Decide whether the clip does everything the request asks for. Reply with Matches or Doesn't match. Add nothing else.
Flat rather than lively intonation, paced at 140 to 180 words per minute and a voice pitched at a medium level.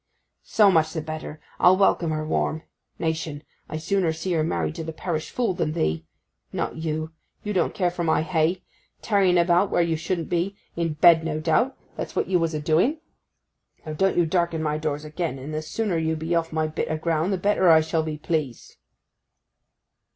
Doesn't match